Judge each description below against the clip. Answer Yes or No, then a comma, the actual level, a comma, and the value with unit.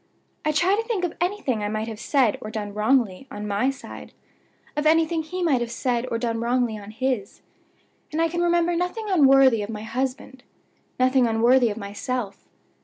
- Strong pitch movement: Yes, wide, 6.2 semitones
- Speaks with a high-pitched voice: Yes, very high, 255 Hz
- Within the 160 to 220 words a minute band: Yes, average, 185 wpm